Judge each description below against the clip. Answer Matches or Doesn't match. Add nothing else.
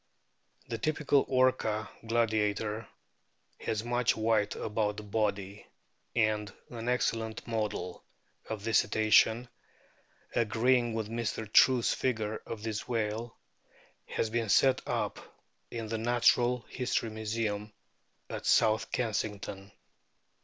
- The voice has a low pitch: Matches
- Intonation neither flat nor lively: Doesn't match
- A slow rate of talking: Matches